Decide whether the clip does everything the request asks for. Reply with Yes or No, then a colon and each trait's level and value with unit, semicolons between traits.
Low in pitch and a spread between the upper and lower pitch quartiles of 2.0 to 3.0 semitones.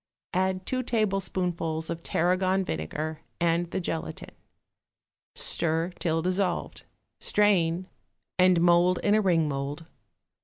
No: medium, 175 Hz; narrow, 2.5 semitones